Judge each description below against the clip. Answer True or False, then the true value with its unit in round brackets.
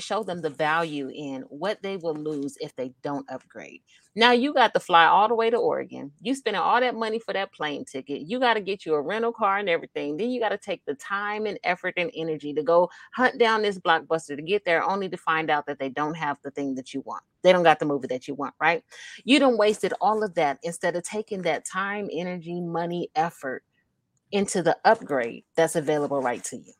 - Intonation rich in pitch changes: True (5.9 semitones)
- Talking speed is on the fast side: True (235 wpm)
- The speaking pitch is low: False (175 Hz)